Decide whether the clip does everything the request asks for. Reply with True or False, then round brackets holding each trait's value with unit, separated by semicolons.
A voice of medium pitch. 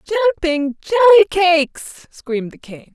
False (345 Hz)